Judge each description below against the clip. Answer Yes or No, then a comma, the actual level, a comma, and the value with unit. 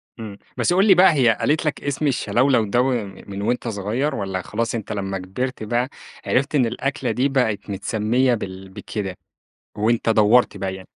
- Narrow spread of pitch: No, average, 4.6 semitones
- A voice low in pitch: Yes, low, 115 Hz